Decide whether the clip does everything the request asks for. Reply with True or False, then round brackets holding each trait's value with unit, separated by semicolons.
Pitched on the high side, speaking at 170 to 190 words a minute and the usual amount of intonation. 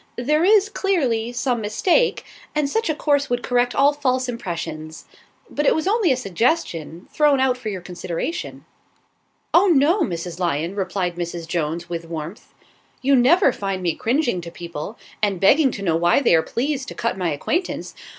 False (235 Hz; 175 wpm; 8.9 semitones)